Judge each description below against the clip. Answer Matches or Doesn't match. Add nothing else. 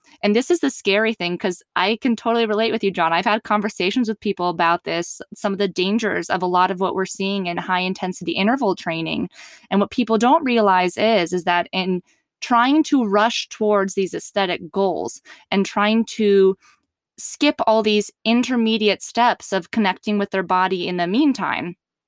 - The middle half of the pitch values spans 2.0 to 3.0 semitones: Doesn't match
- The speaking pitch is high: Matches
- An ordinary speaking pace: Matches